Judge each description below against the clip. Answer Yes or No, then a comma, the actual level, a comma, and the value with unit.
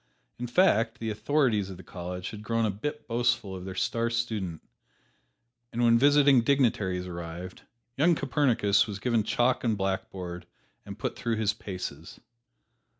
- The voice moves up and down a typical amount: Yes, average, 4.4 semitones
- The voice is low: Yes, low, 110 Hz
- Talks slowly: No, average, 150 wpm